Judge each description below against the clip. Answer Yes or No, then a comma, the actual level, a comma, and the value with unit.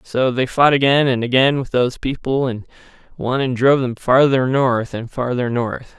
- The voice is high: No, low, 125 Hz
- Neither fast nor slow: Yes, average, 190 wpm